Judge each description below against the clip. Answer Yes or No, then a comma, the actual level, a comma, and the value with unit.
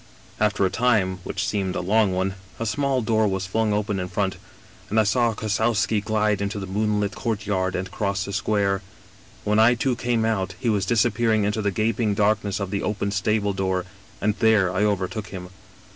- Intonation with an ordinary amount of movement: No, narrow, 2.2 semitones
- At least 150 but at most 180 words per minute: No, average, 195 wpm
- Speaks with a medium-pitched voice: No, low, 105 Hz